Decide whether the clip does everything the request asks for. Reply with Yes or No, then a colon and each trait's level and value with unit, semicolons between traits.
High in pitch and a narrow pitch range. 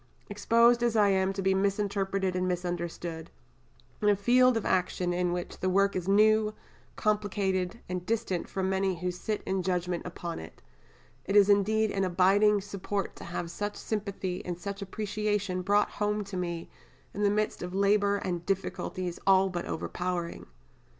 Yes: high, 195 Hz; narrow, 2.3 semitones